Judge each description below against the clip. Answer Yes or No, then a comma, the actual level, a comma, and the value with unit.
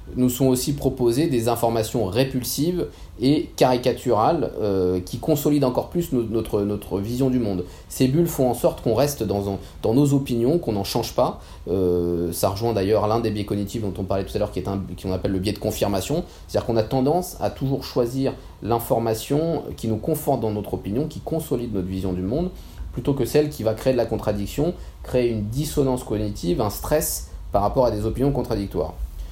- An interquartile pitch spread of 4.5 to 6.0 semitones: Yes, average, 5.3 semitones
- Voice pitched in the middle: No, low, 115 Hz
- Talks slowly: No, average, 205 wpm